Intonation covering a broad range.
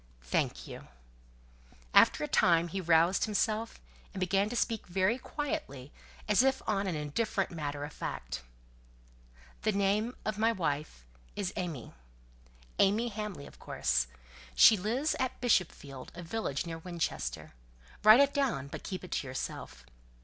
Yes: wide, 6.4 semitones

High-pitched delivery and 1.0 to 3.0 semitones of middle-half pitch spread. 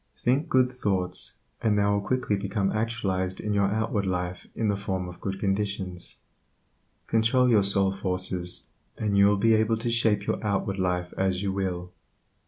No: low, 100 Hz; average, 2.7 semitones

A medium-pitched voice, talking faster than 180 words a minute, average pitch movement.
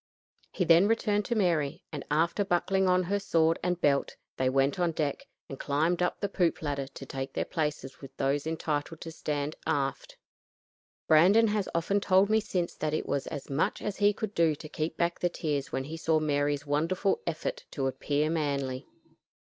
Yes: medium, 160 Hz; average, 190 wpm; average, 4.0 semitones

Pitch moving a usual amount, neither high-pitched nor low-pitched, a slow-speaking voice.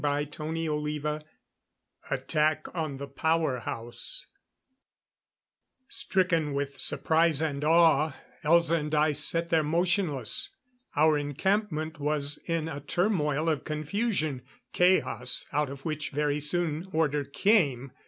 No: narrow, 2.3 semitones; medium, 155 Hz; slow, 115 wpm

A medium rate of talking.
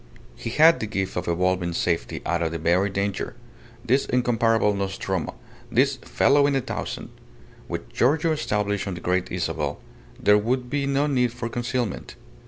Yes: average, 165 wpm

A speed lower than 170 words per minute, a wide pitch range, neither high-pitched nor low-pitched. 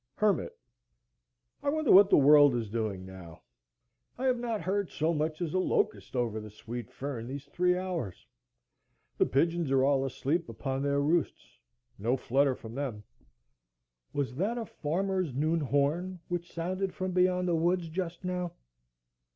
Yes: average, 155 wpm; wide, 5.9 semitones; medium, 155 Hz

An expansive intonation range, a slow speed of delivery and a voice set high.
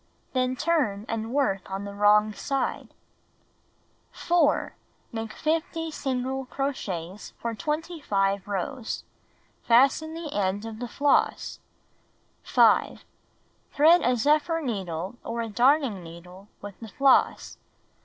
Yes: wide, 6.2 semitones; slow, 115 wpm; high, 235 Hz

